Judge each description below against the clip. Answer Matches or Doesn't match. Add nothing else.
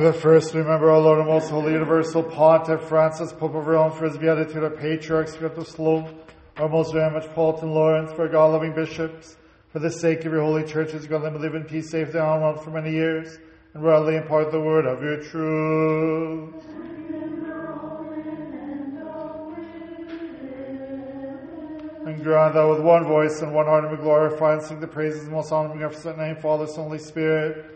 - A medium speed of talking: Matches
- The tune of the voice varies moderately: Doesn't match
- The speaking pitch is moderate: Matches